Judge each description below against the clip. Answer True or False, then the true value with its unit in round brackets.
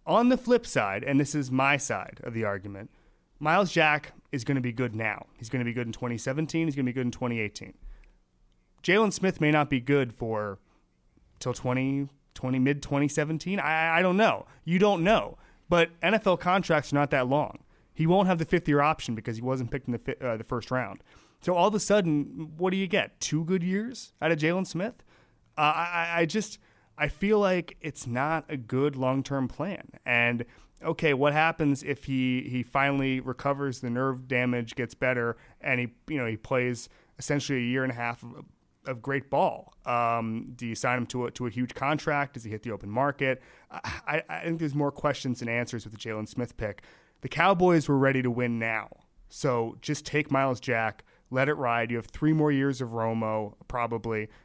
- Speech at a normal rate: False (215 wpm)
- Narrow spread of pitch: False (4.6 semitones)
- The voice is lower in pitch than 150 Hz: True (135 Hz)